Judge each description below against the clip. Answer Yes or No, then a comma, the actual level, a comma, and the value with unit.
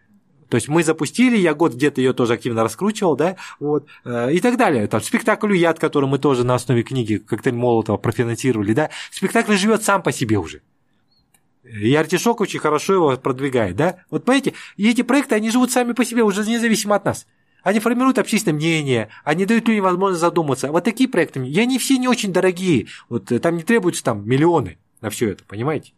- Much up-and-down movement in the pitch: Yes, wide, 8.7 semitones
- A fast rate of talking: Yes, fast, 195 wpm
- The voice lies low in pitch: No, medium, 165 Hz